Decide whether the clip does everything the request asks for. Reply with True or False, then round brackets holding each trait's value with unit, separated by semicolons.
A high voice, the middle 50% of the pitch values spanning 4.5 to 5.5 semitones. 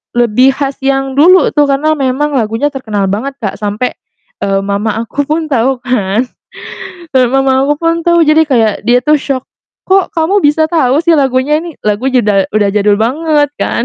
True (270 Hz; 4.8 semitones)